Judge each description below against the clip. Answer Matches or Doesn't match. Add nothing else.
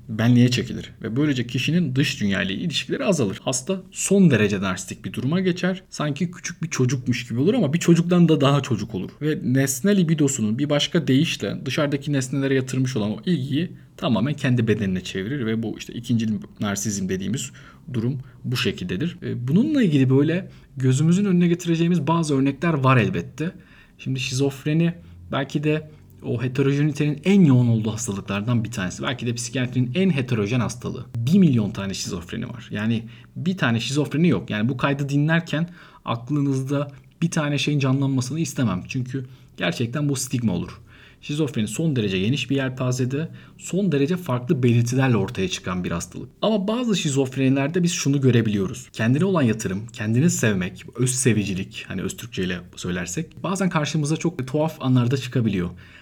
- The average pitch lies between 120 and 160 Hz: Matches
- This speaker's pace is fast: Matches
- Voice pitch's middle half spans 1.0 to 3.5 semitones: Doesn't match